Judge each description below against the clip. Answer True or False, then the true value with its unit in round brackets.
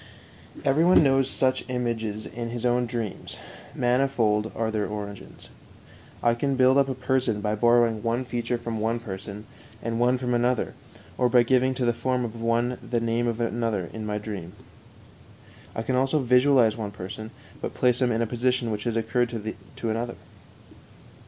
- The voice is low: True (120 Hz)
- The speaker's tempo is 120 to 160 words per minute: False (175 wpm)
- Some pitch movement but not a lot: False (2.2 semitones)